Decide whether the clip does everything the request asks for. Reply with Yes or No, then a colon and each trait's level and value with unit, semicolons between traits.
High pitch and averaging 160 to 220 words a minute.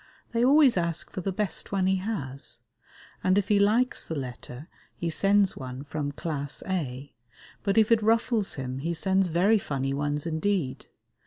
No: medium, 175 Hz; average, 170 wpm